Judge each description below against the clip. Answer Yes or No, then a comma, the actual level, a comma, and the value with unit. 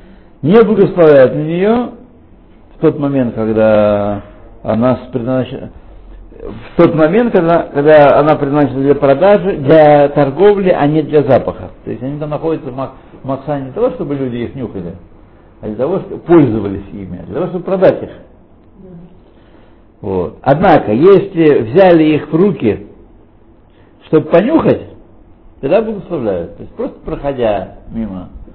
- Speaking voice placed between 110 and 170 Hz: Yes, medium, 140 Hz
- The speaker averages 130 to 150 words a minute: Yes, average, 140 wpm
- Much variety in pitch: Yes, wide, 7.7 semitones